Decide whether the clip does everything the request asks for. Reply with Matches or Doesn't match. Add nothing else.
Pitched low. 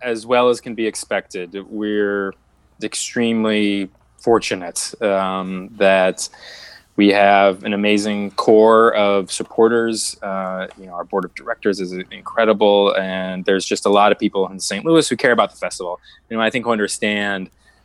Matches